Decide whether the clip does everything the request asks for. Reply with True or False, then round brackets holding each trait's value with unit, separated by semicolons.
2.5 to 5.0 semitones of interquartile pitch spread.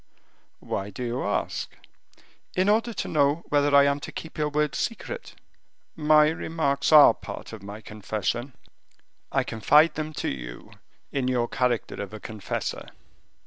False (5.6 semitones)